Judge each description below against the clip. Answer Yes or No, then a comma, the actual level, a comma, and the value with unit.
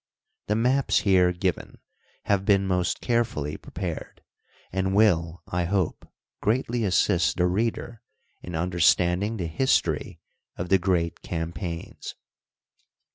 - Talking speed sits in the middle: No, slow, 115 wpm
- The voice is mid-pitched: No, very low, 95 Hz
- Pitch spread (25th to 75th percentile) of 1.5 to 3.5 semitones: Yes, average, 3.2 semitones